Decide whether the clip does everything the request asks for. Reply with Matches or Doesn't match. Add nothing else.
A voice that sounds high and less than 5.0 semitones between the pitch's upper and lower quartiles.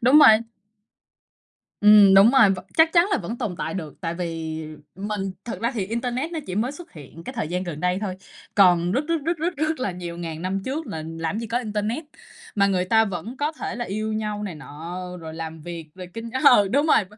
Doesn't match